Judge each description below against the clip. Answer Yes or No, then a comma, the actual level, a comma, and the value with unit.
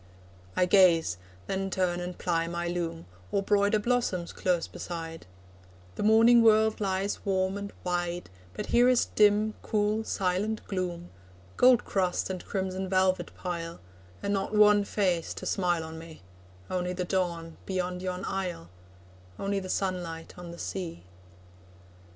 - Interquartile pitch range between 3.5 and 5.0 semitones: No, narrow, 2.6 semitones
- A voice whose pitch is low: No, medium, 185 Hz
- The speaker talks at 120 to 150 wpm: Yes, average, 145 wpm